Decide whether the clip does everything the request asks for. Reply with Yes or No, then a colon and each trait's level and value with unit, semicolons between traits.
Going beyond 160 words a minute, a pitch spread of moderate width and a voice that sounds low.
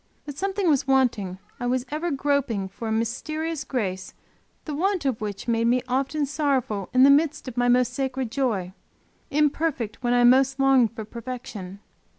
No: average, 175 wpm; average, 3.8 semitones; very high, 255 Hz